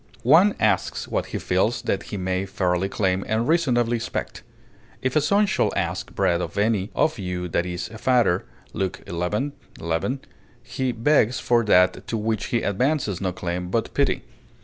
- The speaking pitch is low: Yes, low, 110 Hz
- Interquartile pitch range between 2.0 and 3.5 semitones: No, wide, 5.4 semitones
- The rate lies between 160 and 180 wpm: Yes, average, 170 wpm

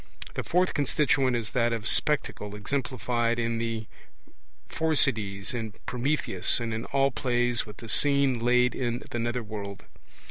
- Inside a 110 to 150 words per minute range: Yes, average, 145 wpm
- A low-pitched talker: Yes, low, 120 Hz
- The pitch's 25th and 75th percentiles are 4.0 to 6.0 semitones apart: No, average, 2.9 semitones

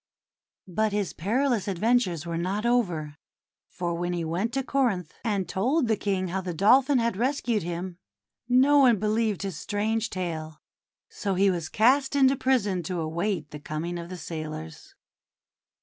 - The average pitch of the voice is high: Yes, high, 195 Hz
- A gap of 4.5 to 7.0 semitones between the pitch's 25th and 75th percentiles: Yes, average, 5.3 semitones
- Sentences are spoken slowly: No, average, 160 wpm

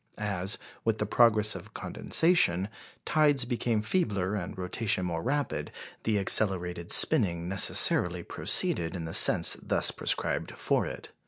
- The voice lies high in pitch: No, low, 105 Hz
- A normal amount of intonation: Yes, average, 4.7 semitones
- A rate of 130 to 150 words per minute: Yes, slow, 135 wpm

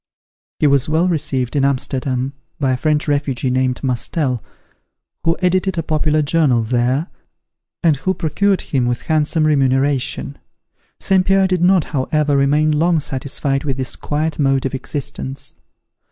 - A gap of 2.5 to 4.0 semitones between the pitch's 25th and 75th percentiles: Yes, average, 3.3 semitones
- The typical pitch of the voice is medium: Yes, medium, 145 Hz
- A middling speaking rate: Yes, average, 150 wpm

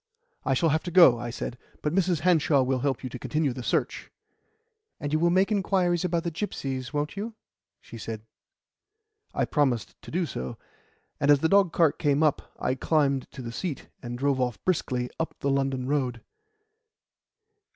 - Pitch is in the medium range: Yes, medium, 145 Hz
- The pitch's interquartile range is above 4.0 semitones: Yes, average, 4.9 semitones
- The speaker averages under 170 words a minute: No, average, 185 wpm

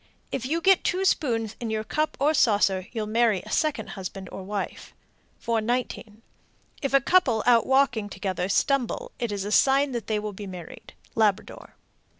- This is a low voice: No, high, 225 Hz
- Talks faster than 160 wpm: Yes, average, 170 wpm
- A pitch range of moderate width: Yes, average, 4.8 semitones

